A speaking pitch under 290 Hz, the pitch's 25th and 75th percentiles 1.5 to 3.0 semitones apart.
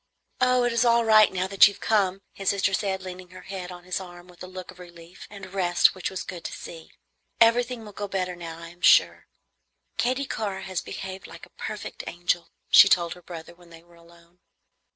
Yes: medium, 185 Hz; narrow, 2.5 semitones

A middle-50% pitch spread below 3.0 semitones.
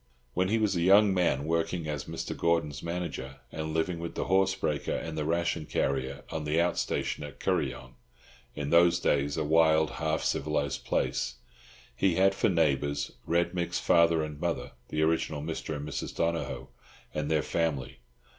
Yes: narrow, 2.5 semitones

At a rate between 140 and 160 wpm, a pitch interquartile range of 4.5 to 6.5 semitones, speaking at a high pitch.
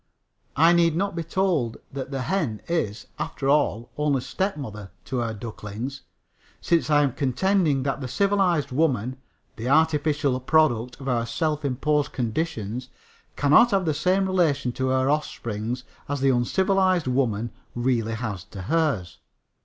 No: average, 145 wpm; average, 5.0 semitones; medium, 140 Hz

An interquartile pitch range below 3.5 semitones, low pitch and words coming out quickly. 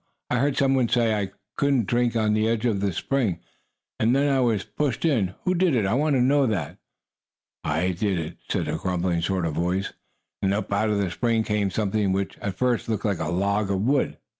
No: average, 4.4 semitones; low, 105 Hz; fast, 225 wpm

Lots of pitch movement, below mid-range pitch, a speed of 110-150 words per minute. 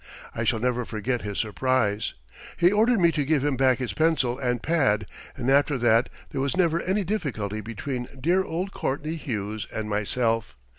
No: wide, 6.2 semitones; low, 130 Hz; average, 180 wpm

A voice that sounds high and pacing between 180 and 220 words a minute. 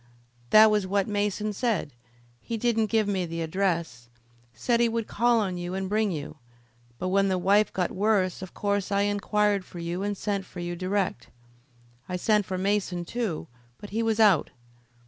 Yes: high, 200 Hz; average, 185 wpm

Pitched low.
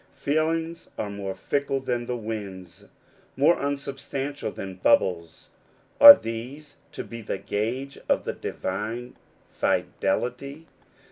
Yes: low, 125 Hz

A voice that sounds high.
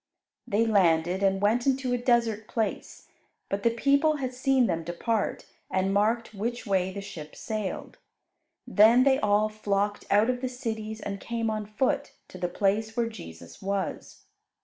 Yes: high, 215 Hz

